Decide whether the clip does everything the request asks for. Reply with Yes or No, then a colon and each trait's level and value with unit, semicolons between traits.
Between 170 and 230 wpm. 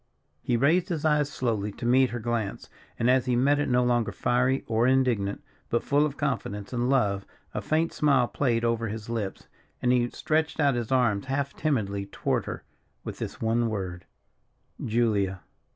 Yes: average, 180 wpm